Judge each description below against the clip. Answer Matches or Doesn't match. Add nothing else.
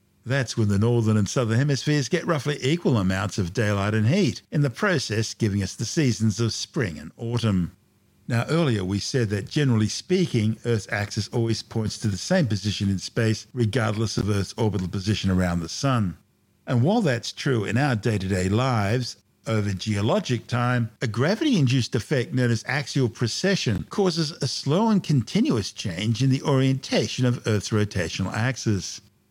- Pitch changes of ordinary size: Matches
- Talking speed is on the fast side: Doesn't match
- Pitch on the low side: Matches